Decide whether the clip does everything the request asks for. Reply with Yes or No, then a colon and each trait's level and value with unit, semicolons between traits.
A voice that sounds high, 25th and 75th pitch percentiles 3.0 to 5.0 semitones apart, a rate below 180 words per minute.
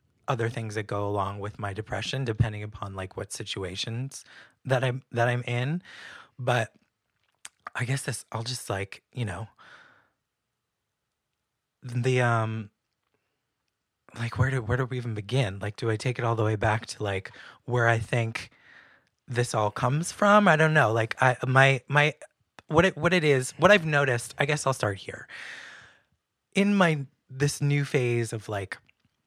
No: low, 120 Hz; average, 3.8 semitones; average, 170 wpm